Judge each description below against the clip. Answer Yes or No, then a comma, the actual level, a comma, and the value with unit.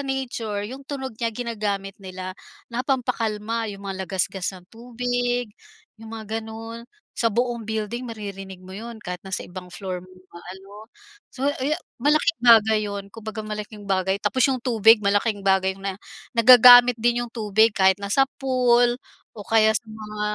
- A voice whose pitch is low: No, high, 220 Hz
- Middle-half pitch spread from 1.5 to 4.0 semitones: Yes, average, 3.4 semitones